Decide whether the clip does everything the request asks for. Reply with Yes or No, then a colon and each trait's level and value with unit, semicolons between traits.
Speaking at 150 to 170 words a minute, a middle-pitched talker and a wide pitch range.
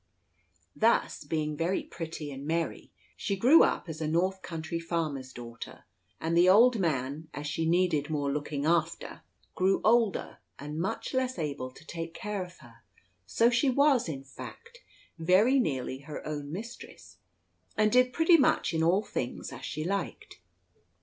Yes: average, 155 wpm; medium, 165 Hz; wide, 6.0 semitones